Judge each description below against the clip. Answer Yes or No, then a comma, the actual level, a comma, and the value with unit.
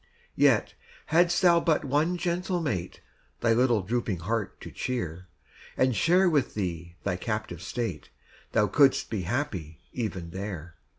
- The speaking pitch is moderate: No, low, 115 Hz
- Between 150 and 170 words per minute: No, average, 140 wpm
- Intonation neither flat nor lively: No, wide, 8.5 semitones